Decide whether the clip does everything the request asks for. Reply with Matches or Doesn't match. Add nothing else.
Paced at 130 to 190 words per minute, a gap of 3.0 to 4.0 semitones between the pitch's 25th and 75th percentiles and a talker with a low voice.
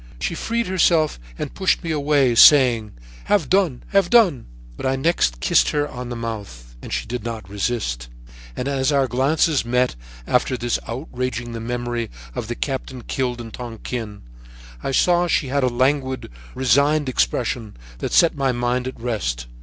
Matches